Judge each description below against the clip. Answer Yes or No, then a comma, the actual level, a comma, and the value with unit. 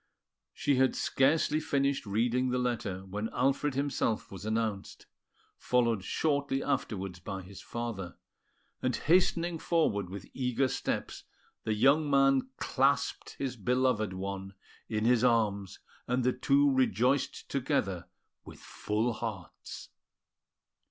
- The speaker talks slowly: Yes, slow, 120 wpm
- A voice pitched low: Yes, low, 125 Hz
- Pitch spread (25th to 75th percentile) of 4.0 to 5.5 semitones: Yes, average, 5.0 semitones